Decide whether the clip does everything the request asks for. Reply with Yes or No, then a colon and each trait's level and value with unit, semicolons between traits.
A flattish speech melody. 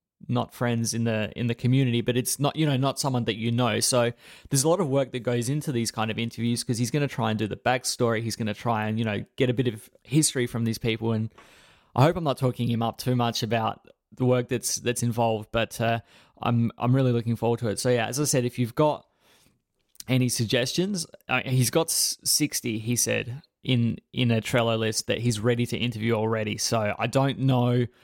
Yes: narrow, 1.9 semitones